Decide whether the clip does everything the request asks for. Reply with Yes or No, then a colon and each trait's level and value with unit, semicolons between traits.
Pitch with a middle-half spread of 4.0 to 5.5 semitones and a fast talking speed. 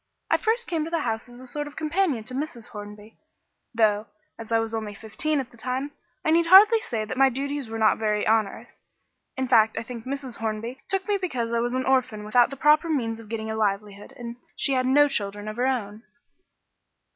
Yes: average, 4.4 semitones; fast, 220 wpm